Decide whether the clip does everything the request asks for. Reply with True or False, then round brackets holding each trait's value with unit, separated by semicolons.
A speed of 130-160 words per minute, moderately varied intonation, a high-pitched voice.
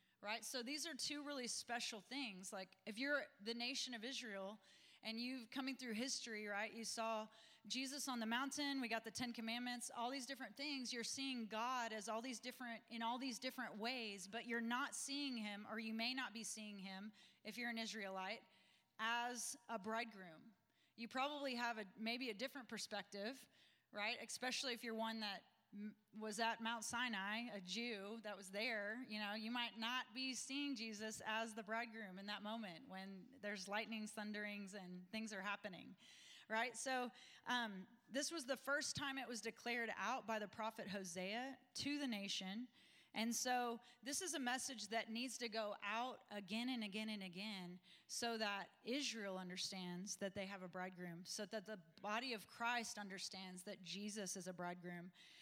False (180 wpm; 3.1 semitones; 225 Hz)